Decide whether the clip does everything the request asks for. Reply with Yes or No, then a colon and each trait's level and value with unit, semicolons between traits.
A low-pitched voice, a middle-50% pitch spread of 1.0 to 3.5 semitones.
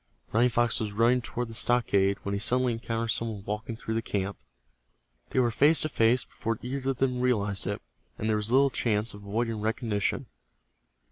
Yes: low, 115 Hz; average, 2.8 semitones